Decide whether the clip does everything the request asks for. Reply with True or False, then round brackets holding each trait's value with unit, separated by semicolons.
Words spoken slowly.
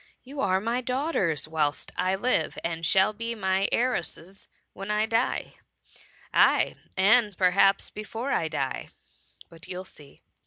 False (145 wpm)